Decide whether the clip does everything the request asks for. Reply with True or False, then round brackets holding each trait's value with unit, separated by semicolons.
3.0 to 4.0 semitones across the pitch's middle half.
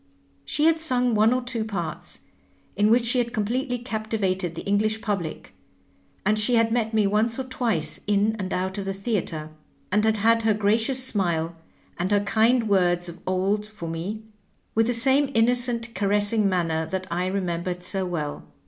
True (3.7 semitones)